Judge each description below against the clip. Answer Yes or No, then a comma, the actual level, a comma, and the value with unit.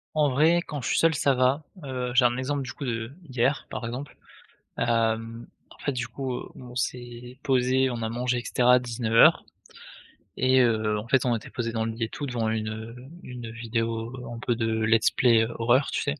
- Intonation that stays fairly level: Yes, narrow, 2.3 semitones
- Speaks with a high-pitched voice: No, low, 120 Hz